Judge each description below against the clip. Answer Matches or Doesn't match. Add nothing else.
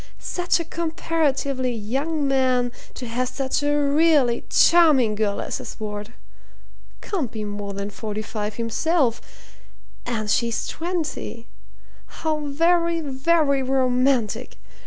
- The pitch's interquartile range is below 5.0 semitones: Doesn't match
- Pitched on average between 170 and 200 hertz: Doesn't match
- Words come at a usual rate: Doesn't match